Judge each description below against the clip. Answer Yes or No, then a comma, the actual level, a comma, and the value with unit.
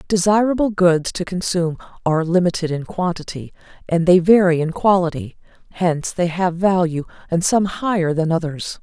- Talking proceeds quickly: No, average, 150 wpm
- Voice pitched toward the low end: No, medium, 175 Hz